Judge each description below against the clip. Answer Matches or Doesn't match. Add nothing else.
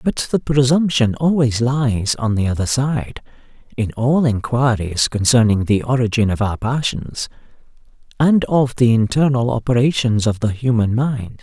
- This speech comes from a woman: Doesn't match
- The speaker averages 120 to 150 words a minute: Matches